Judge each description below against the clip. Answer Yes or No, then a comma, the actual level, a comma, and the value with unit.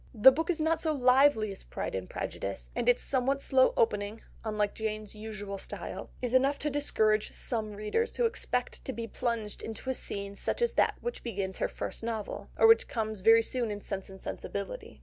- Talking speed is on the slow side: No, average, 200 wpm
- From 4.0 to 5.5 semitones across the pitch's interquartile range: Yes, average, 4.3 semitones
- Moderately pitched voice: No, high, 225 Hz